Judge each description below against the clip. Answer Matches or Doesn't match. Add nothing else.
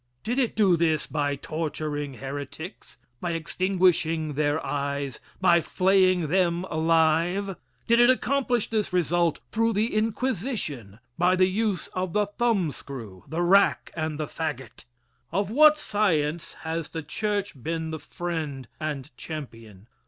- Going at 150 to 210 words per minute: Doesn't match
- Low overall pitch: Doesn't match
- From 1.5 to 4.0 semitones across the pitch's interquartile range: Doesn't match